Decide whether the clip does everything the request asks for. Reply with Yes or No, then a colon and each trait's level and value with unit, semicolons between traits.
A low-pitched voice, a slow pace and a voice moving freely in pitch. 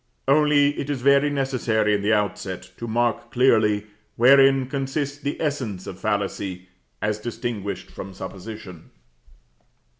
No: low, 115 Hz; slow, 125 wpm; average, 5.0 semitones